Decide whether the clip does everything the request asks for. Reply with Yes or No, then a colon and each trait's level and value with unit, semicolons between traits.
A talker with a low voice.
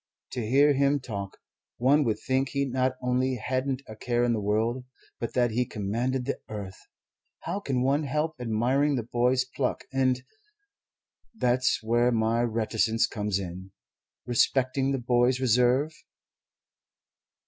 Yes: low, 125 Hz